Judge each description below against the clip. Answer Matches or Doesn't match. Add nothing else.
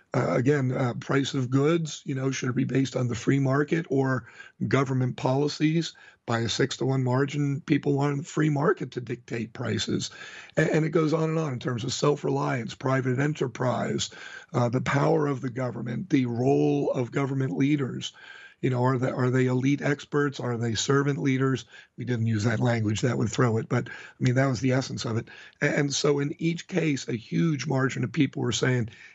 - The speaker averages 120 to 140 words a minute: Doesn't match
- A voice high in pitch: Doesn't match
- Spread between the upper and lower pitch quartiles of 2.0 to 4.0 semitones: Matches